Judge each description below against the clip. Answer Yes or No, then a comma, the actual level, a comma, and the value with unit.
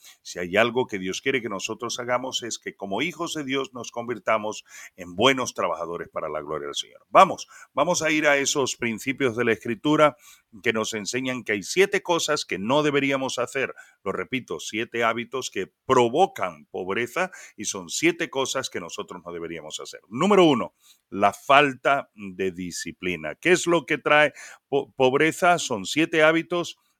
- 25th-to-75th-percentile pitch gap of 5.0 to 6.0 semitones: Yes, wide, 5.5 semitones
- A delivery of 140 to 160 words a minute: No, average, 175 wpm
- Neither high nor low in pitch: No, low, 130 Hz